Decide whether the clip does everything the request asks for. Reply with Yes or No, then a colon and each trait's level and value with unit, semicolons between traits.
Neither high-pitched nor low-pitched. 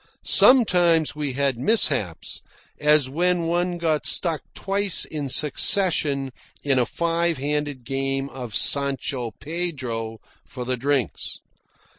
Yes: medium, 145 Hz